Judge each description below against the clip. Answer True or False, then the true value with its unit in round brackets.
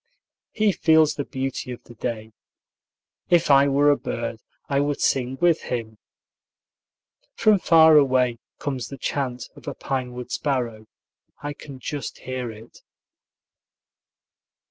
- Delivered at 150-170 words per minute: False (135 wpm)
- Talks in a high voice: False (135 Hz)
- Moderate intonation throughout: True (3.0 semitones)